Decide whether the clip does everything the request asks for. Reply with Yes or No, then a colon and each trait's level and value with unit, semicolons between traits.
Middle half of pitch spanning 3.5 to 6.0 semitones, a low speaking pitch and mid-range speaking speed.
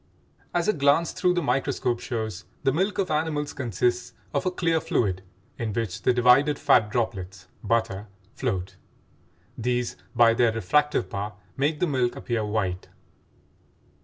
Yes: average, 5.2 semitones; low, 120 Hz; average, 145 wpm